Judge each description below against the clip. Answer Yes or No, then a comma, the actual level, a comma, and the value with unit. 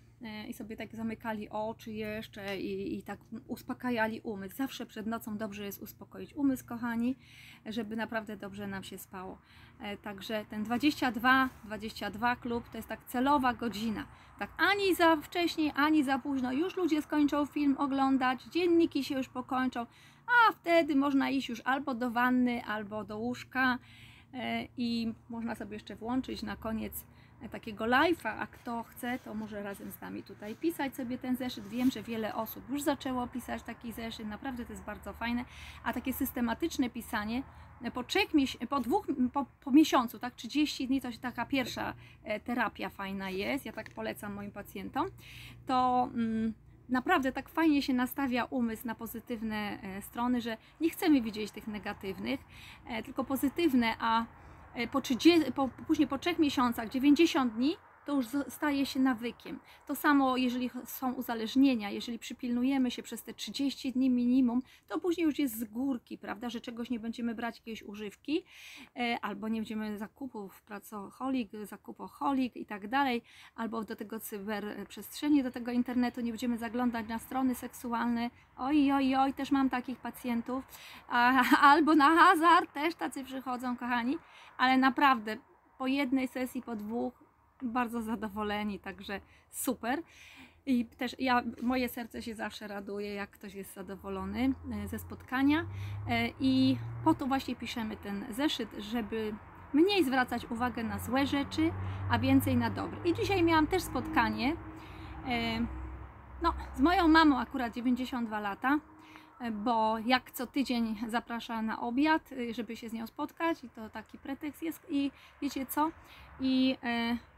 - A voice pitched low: No, high, 245 Hz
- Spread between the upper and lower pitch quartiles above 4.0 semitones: No, average, 3.5 semitones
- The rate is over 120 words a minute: Yes, average, 150 wpm